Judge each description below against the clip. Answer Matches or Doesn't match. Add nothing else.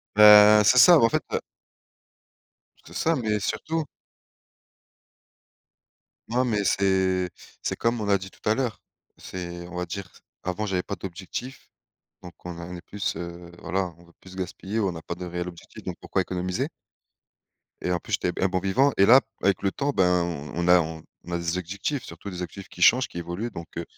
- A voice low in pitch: Matches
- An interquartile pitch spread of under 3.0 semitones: Doesn't match